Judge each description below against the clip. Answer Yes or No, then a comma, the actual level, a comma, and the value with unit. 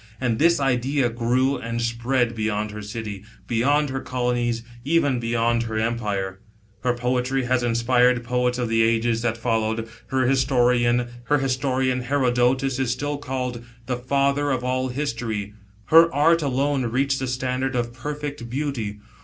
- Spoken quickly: No, average, 145 wpm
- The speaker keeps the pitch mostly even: Yes, narrow, 2.3 semitones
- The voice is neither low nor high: No, low, 125 Hz